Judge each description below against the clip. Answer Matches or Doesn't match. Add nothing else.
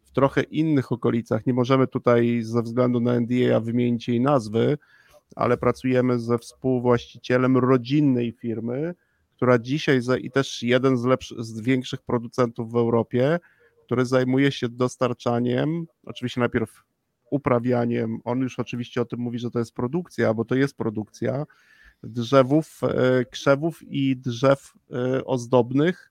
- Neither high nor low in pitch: Doesn't match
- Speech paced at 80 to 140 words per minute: Matches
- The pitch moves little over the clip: Matches